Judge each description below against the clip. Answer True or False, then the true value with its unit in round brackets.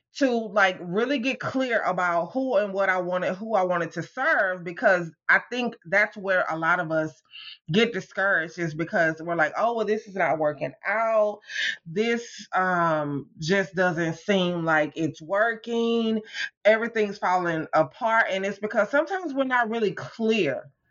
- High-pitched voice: True (195 Hz)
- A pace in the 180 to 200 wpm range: False (165 wpm)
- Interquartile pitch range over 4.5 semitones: True (4.9 semitones)